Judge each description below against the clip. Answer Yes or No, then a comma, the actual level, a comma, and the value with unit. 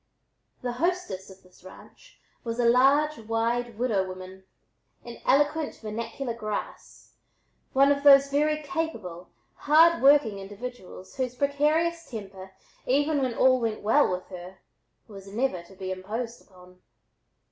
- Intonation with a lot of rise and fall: Yes, wide, 6.5 semitones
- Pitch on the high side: Yes, high, 235 Hz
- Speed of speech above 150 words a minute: No, slow, 135 wpm